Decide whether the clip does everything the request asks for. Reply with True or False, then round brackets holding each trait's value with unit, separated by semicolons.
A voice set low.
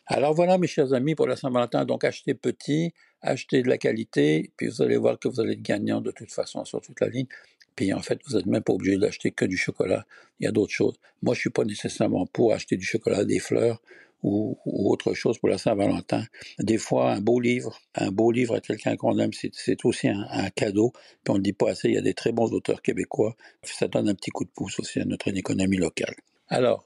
True (120 Hz)